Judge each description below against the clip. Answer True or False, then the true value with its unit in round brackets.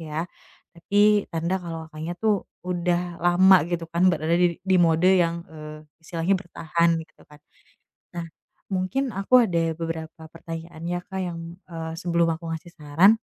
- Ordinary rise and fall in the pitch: False (2.0 semitones)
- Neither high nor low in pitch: True (170 Hz)